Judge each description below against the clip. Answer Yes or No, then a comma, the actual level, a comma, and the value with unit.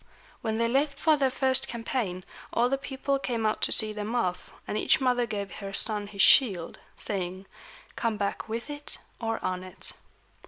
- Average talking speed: Yes, average, 185 wpm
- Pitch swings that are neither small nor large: Yes, average, 4.6 semitones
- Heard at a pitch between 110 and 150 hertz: No, high, 225 Hz